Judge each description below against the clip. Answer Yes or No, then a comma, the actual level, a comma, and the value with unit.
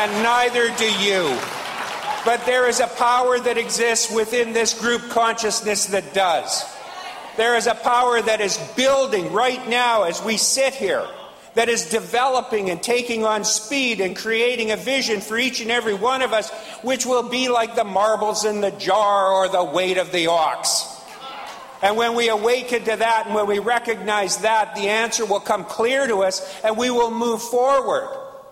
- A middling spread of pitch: No, narrow, 2.3 semitones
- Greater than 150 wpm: Yes, average, 180 wpm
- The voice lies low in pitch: No, high, 230 Hz